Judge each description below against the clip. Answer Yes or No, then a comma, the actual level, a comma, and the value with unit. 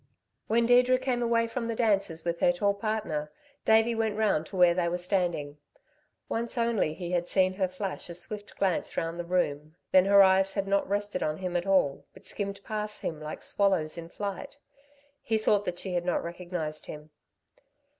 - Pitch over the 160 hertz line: Yes, high, 190 Hz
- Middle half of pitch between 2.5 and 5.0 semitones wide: Yes, average, 3.8 semitones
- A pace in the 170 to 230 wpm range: Yes, average, 195 wpm